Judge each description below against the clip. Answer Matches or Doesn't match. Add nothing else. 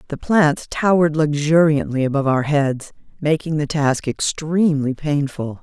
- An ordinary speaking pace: Doesn't match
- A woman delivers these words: Matches